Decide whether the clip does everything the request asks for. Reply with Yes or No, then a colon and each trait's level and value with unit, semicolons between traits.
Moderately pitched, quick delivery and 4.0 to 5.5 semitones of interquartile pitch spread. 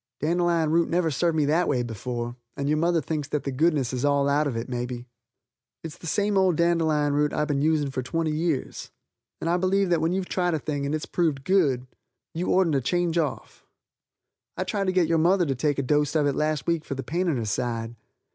No: medium, 155 Hz; fast, 235 wpm; average, 3.6 semitones